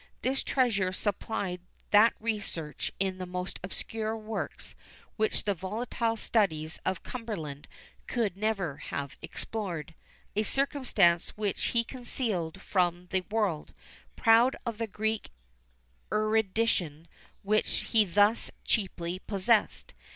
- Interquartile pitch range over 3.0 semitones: Yes, average, 3.8 semitones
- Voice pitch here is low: No, high, 205 Hz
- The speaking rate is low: Yes, slow, 115 wpm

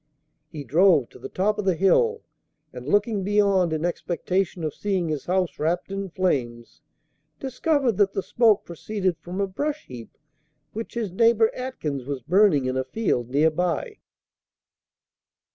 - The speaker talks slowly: No, average, 155 wpm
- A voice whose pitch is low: No, medium, 185 Hz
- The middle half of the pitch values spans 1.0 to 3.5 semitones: No, average, 5.0 semitones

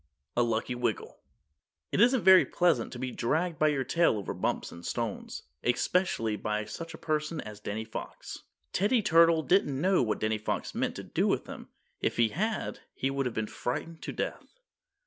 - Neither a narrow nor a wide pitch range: No, wide, 7.2 semitones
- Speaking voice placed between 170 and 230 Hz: No, low, 135 Hz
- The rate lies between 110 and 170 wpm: No, average, 185 wpm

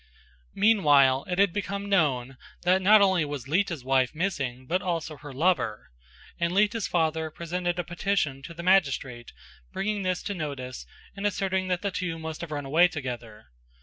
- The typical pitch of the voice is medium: Yes, medium, 170 Hz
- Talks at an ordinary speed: Yes, average, 170 wpm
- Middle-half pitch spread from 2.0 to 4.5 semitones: No, average, 5.3 semitones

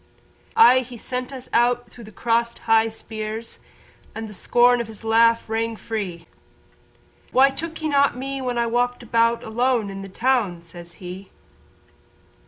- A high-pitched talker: Yes, high, 230 Hz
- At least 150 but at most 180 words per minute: Yes, average, 160 wpm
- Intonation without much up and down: Yes, narrow, 2.2 semitones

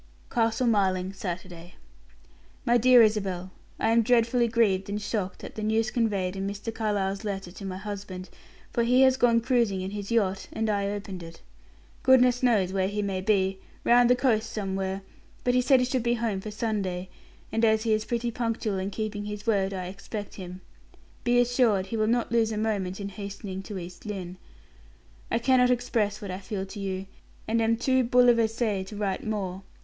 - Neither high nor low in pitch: No, high, 210 Hz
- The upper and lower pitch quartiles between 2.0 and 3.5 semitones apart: Yes, average, 3.2 semitones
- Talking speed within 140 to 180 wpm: No, average, 190 wpm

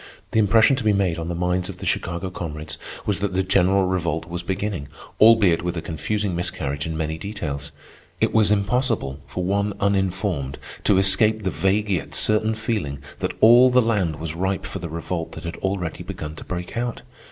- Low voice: Yes, very low, 95 Hz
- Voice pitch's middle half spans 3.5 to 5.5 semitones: Yes, average, 4.0 semitones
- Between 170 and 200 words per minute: Yes, average, 195 wpm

